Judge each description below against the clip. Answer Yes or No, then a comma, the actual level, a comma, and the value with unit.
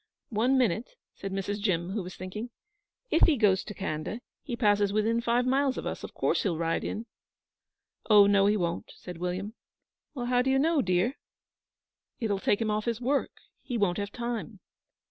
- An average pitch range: Yes, average, 4.0 semitones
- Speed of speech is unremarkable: Yes, average, 185 wpm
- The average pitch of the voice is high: Yes, high, 210 Hz